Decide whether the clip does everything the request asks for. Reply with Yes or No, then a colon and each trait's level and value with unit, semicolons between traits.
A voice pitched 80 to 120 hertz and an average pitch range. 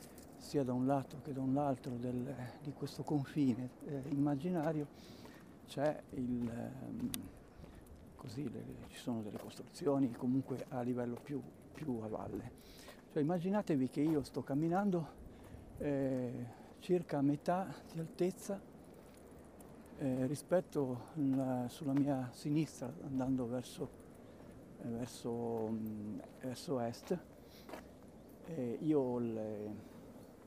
No: low, 135 Hz; average, 3.1 semitones